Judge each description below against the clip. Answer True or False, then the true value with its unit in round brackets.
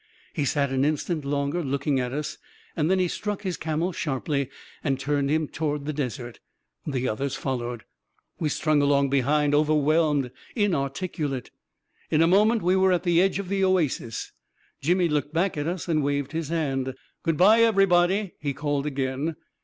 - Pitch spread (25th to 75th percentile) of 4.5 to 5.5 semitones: False (3.9 semitones)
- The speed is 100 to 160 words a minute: False (180 wpm)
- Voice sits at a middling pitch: True (150 Hz)